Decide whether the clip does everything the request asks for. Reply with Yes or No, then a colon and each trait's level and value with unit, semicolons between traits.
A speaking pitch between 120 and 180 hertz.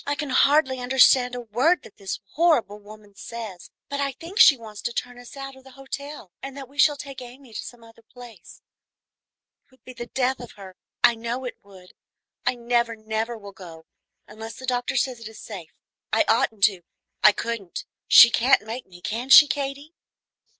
No: high, 240 Hz